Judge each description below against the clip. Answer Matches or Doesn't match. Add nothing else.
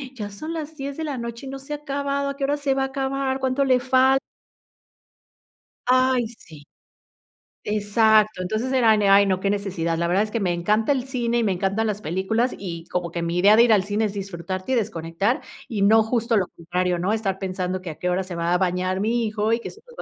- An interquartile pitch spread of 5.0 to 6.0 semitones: Matches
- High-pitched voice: Matches